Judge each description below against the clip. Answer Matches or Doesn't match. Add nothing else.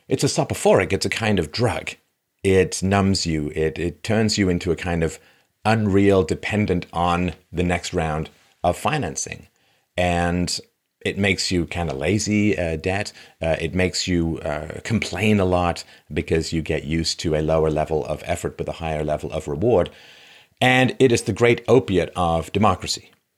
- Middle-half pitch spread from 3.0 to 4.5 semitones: Matches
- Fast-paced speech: Doesn't match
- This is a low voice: Matches